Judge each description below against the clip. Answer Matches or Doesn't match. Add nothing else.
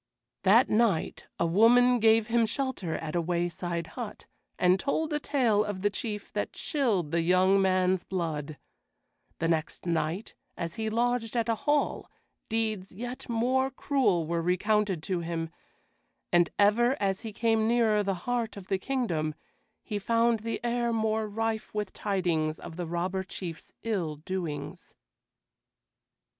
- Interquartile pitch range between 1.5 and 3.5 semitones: Doesn't match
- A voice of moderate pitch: Doesn't match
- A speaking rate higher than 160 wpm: Doesn't match